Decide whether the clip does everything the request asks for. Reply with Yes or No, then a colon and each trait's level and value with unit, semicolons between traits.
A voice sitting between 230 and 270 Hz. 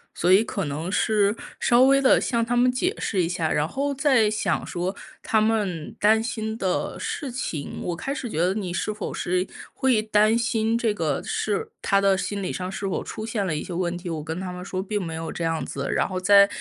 No: high, 200 Hz